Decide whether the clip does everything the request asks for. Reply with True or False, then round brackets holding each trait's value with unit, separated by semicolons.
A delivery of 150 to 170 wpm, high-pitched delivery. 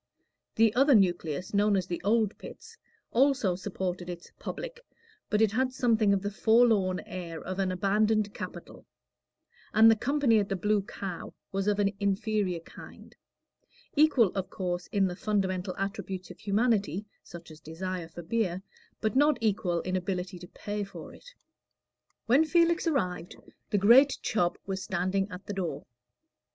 True (160 wpm; 200 Hz)